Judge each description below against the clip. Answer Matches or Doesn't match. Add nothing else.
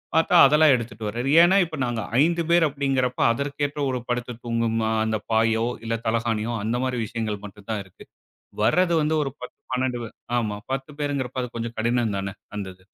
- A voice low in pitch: Matches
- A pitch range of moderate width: Matches